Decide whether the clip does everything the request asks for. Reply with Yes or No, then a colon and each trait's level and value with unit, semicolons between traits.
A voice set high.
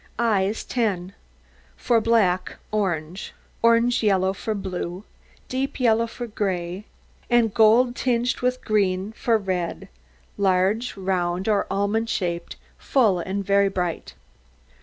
Yes: high, 200 Hz